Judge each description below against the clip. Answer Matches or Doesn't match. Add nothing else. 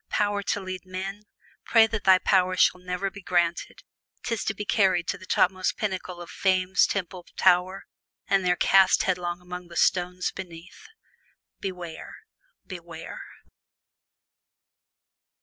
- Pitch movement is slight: Matches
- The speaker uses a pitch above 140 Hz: Matches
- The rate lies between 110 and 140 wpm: Matches